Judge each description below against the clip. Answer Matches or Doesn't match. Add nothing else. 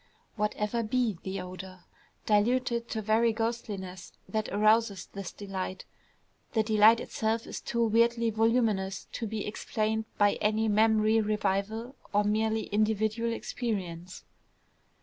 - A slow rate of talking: Matches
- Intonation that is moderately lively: Doesn't match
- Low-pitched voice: Doesn't match